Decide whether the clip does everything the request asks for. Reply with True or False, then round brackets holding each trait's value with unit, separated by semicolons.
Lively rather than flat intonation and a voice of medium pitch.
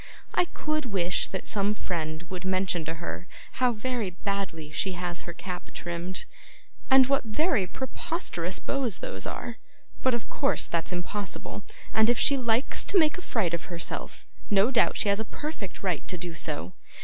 False (5.9 semitones; 195 Hz)